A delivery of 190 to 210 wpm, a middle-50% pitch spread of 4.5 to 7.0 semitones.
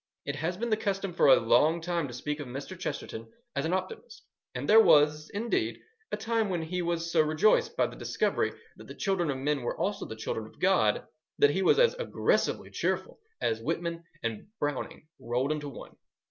Yes: average, 200 wpm; average, 5.1 semitones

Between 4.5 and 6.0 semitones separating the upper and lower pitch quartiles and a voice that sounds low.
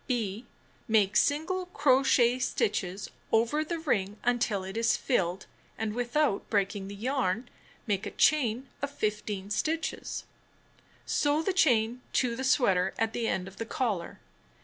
No: average, 5.2 semitones; high, 230 Hz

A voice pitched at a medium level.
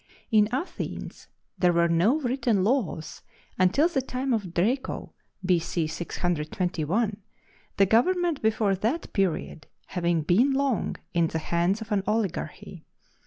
No: high, 200 Hz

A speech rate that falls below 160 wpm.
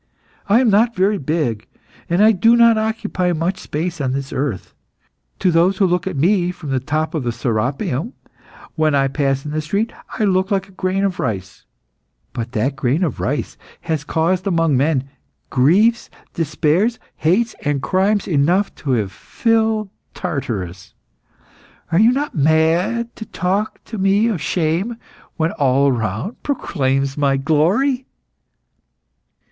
Yes: average, 150 wpm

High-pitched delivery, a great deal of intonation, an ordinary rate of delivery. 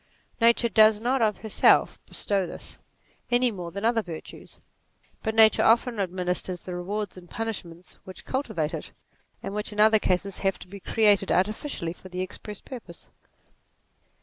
No: high, 205 Hz; average, 3.5 semitones; average, 160 wpm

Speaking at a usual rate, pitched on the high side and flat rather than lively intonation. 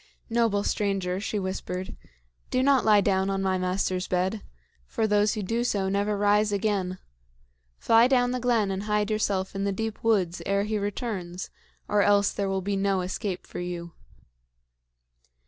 Yes: average, 165 wpm; high, 200 Hz; narrow, 2.0 semitones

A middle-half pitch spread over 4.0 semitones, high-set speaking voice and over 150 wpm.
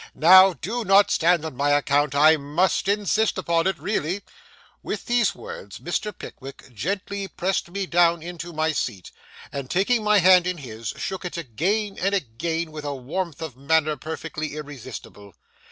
No: average, 4.8 semitones; medium, 170 Hz; average, 165 wpm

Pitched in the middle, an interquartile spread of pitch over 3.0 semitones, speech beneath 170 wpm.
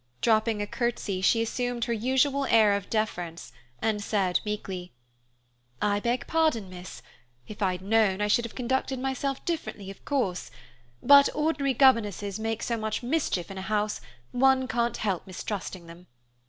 No: high, 220 Hz; average, 4.3 semitones; average, 155 wpm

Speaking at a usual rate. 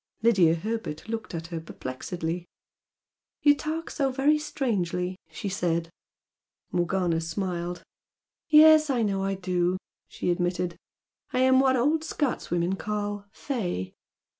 No: slow, 120 wpm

